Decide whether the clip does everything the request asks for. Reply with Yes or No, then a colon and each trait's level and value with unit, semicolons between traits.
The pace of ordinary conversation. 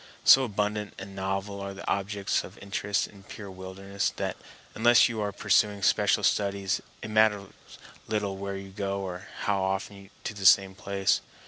Yes: average, 170 wpm